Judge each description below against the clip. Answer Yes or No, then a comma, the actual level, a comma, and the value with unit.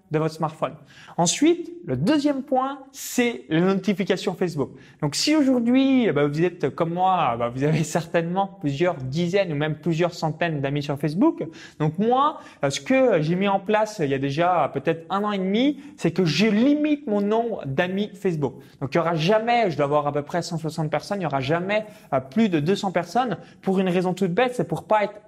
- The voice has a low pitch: No, medium, 185 Hz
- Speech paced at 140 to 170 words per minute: No, average, 205 wpm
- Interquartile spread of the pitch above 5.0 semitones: Yes, wide, 5.6 semitones